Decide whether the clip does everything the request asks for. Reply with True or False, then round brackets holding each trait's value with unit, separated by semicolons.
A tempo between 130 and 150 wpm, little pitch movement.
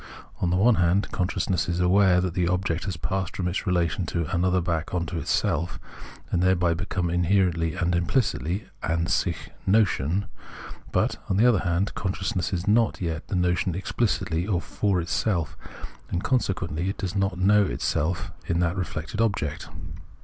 False (165 wpm; 2.2 semitones)